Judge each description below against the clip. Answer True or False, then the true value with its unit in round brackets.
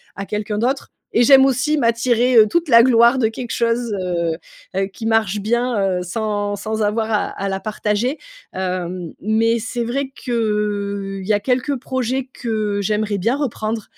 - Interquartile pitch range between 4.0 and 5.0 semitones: False (2.9 semitones)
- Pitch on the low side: False (220 Hz)